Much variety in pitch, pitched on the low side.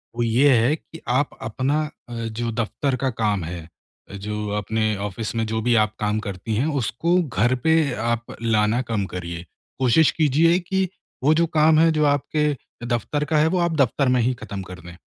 Yes: wide, 5.8 semitones; low, 120 Hz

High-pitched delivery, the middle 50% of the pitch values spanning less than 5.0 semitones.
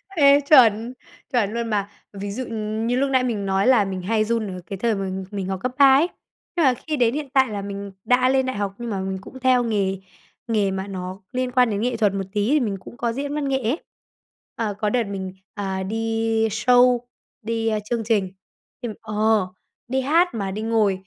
Yes: high, 225 Hz; average, 3.9 semitones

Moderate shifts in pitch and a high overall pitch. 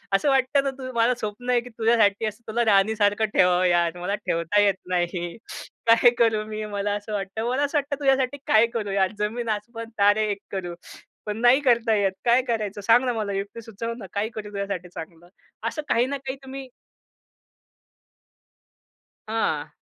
Yes: average, 3.3 semitones; high, 220 Hz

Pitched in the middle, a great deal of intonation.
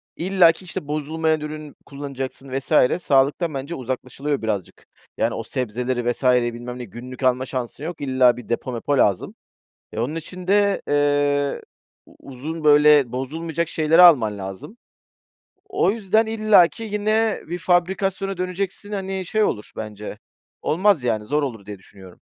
Yes: medium, 145 Hz; wide, 6.1 semitones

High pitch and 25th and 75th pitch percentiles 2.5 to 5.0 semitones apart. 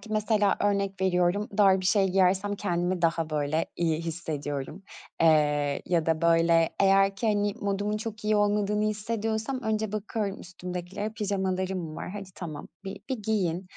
Yes: high, 195 Hz; average, 3.5 semitones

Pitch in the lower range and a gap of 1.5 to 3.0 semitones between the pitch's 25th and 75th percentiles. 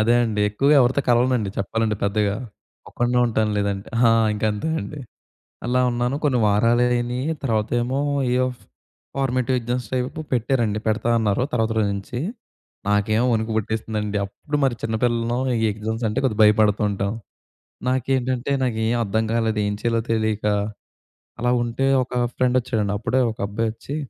Yes: low, 115 Hz; average, 2.7 semitones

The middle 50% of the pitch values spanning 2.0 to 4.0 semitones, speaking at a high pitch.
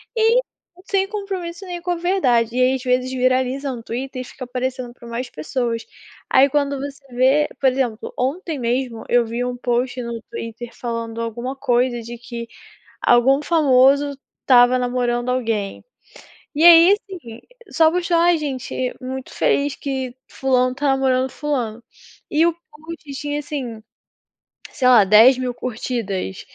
Yes: average, 3.2 semitones; very high, 255 Hz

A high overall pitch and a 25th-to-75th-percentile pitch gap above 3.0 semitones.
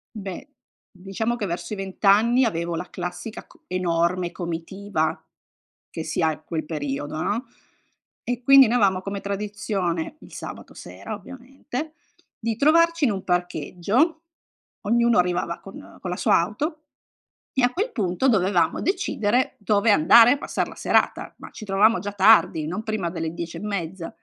Yes: high, 200 Hz; average, 5.1 semitones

